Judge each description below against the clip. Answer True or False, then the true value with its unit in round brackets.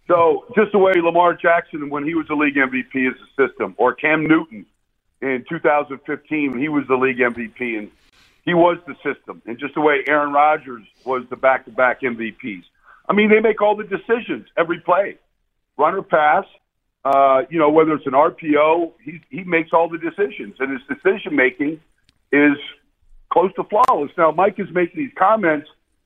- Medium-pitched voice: True (150 Hz)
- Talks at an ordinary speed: True (185 wpm)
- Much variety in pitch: False (4.6 semitones)